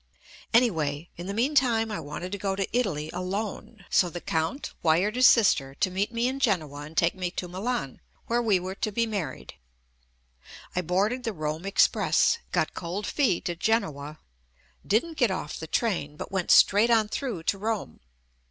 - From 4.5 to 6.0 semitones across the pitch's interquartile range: Yes, average, 5.2 semitones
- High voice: Yes, high, 195 Hz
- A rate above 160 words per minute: Yes, average, 180 wpm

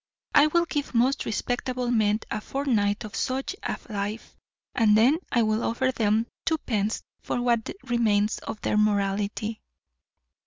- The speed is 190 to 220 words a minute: No, average, 145 wpm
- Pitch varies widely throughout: No, average, 3.2 semitones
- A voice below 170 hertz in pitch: No, high, 225 Hz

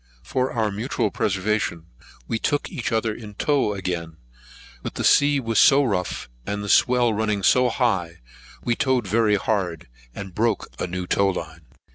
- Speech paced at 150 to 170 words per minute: Yes, average, 165 wpm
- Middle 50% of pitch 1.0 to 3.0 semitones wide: No, average, 4.2 semitones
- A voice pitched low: Yes, low, 105 Hz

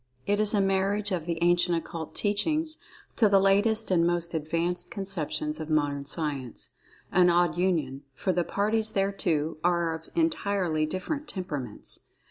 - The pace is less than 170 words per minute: Yes, average, 145 wpm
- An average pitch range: Yes, average, 4.0 semitones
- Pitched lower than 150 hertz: No, medium, 175 Hz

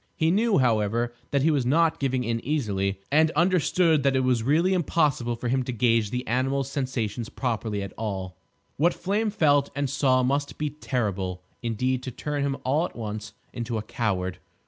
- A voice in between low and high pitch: No, low, 130 Hz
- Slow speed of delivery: No, average, 185 wpm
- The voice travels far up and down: No, average, 4.5 semitones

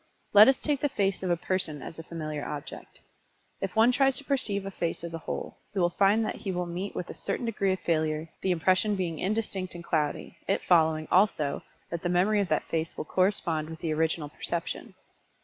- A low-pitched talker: No, medium, 180 Hz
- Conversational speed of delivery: No, fast, 220 wpm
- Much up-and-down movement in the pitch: No, average, 3.6 semitones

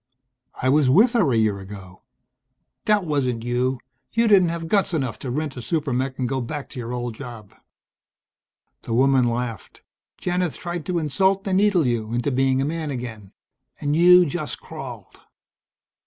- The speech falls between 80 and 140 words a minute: No, average, 170 wpm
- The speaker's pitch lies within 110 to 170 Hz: Yes, low, 135 Hz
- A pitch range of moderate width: No, wide, 5.9 semitones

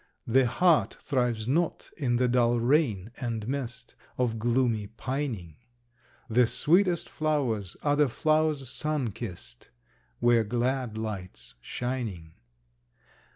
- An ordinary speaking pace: No, slow, 110 wpm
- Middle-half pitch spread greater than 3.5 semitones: Yes, average, 4.0 semitones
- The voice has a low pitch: Yes, low, 120 Hz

